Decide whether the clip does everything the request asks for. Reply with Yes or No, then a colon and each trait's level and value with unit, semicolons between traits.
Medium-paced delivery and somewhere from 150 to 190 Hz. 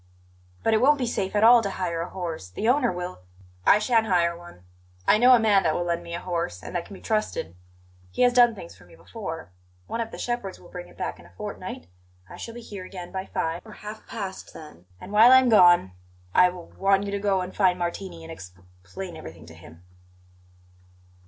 No: fast, 235 wpm; medium, 185 Hz